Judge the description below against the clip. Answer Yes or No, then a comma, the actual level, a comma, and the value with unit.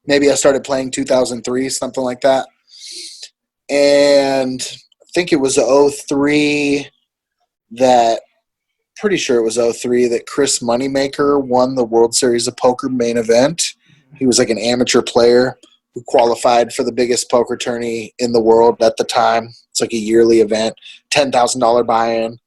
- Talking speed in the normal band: Yes, average, 160 wpm